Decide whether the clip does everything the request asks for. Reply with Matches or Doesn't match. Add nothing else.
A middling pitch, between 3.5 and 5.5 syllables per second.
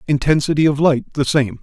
Matches